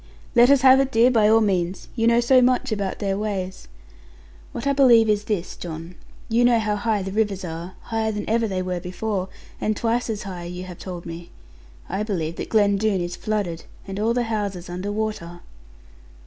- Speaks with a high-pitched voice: Yes, high, 210 Hz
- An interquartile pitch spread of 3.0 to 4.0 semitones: Yes, average, 3.6 semitones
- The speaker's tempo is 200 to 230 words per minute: Yes, fast, 205 wpm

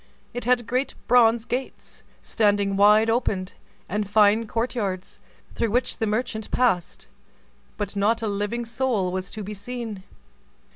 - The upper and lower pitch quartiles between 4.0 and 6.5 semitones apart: No, average, 2.7 semitones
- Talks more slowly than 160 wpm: Yes, average, 145 wpm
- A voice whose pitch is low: No, high, 220 Hz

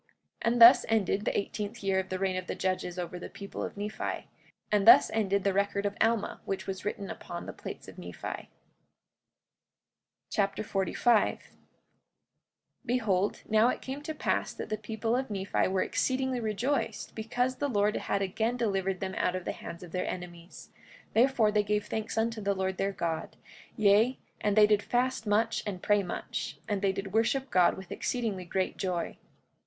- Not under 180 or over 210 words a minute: Yes, average, 185 wpm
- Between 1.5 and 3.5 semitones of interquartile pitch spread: Yes, average, 3.0 semitones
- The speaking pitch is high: Yes, high, 205 Hz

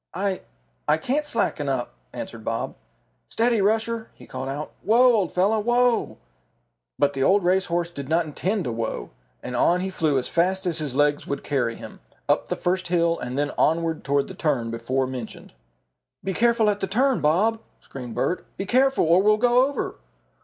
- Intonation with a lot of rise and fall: Yes, wide, 7.2 semitones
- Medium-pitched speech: Yes, medium, 175 Hz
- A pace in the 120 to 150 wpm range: No, average, 190 wpm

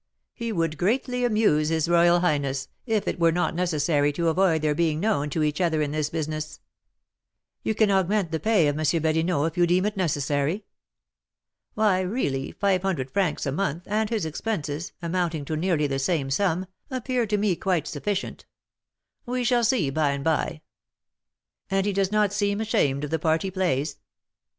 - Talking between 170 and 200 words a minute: Yes, average, 180 wpm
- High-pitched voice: No, medium, 170 Hz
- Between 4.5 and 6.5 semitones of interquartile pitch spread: Yes, average, 4.8 semitones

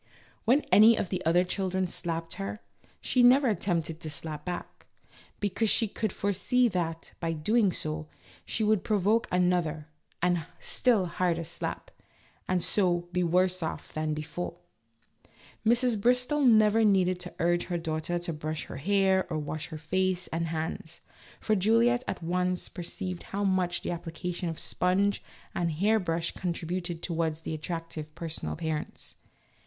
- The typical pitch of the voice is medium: Yes, medium, 180 Hz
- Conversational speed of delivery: Yes, average, 155 wpm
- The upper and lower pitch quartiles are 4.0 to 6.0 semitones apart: No, average, 3.5 semitones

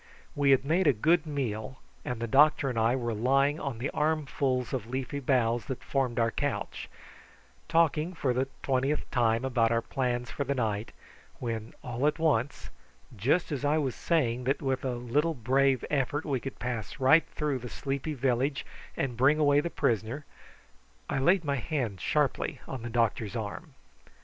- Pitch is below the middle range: Yes, low, 130 Hz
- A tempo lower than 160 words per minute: No, average, 175 wpm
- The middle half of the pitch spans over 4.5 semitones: No, average, 3.4 semitones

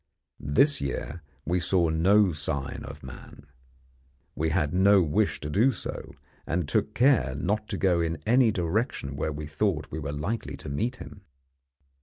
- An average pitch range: No, wide, 5.7 semitones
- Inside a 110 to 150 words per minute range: No, average, 165 wpm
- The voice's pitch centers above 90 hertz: No, very low, 85 Hz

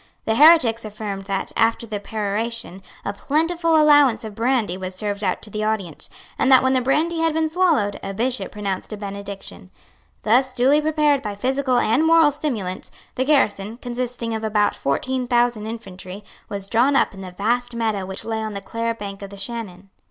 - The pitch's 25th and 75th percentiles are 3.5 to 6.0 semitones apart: Yes, average, 4.5 semitones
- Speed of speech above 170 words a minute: Yes, average, 190 wpm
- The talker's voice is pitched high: Yes, high, 225 Hz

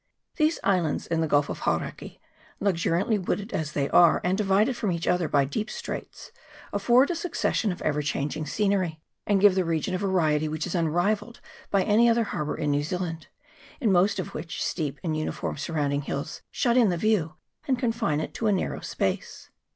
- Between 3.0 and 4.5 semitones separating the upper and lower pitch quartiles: No, average, 5.1 semitones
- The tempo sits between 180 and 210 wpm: Yes, average, 190 wpm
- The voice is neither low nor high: Yes, medium, 180 Hz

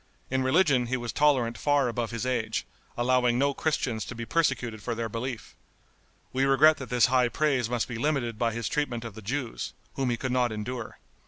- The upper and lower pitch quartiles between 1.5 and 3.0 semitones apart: Yes, narrow, 2.5 semitones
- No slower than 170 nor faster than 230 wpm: Yes, average, 200 wpm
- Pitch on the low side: Yes, low, 125 Hz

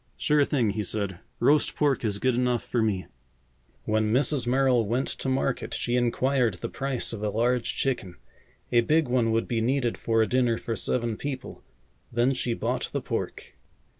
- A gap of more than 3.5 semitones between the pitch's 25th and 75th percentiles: No, average, 2.7 semitones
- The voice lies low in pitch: Yes, low, 120 Hz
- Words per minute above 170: Yes, average, 180 wpm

